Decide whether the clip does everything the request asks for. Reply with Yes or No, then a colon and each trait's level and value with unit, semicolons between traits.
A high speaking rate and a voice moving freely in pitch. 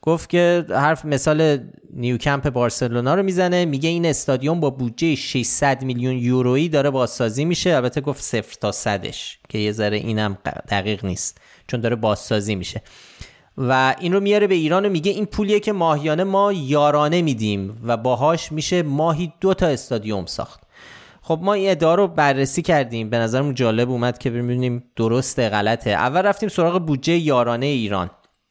Yes: fast, 160 wpm; wide, 5.9 semitones